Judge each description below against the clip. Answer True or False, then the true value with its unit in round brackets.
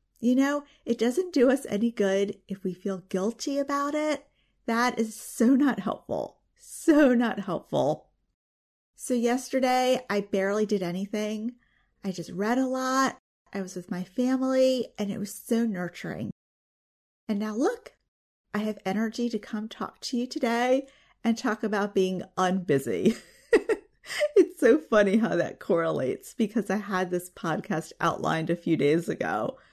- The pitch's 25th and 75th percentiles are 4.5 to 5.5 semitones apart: True (5.0 semitones)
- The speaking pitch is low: False (220 Hz)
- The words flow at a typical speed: True (155 wpm)